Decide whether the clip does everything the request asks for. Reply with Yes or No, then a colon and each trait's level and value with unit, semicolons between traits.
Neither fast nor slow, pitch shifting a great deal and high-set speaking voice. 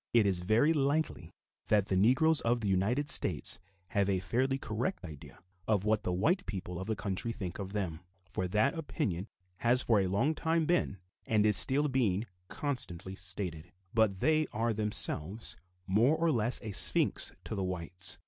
No: average, 175 wpm; wide, 5.7 semitones; low, 105 Hz